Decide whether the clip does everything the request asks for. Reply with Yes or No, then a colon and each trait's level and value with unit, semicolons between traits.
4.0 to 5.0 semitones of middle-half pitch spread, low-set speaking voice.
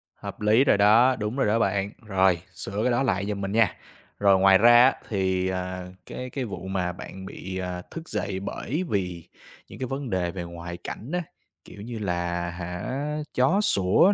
Yes: average, 4.4 semitones; low, 100 Hz